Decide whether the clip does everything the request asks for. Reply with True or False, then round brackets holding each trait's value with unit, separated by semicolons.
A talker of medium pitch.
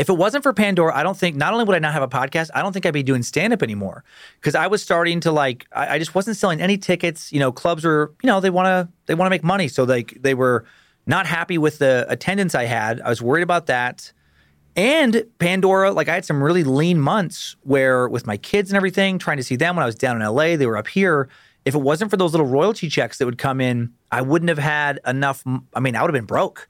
True (155 Hz)